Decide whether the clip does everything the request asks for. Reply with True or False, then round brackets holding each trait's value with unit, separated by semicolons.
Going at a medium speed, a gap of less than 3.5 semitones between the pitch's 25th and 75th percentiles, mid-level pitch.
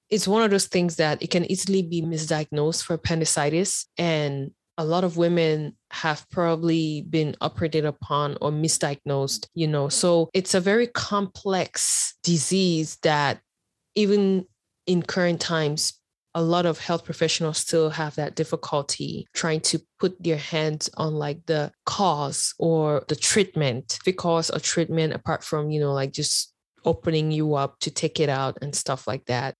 True (160 wpm; 2.5 semitones; 160 Hz)